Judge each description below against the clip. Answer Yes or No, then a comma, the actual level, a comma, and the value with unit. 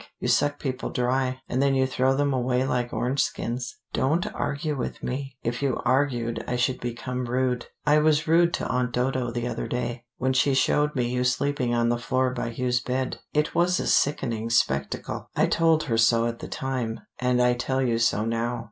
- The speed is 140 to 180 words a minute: No, average, 200 wpm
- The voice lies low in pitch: Yes, low, 125 Hz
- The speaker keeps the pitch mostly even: Yes, narrow, 2.0 semitones